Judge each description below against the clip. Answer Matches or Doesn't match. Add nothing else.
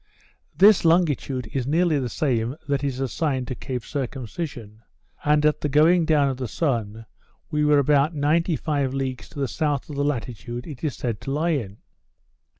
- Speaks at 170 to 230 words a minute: Matches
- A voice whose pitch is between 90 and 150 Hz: Matches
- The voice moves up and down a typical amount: Matches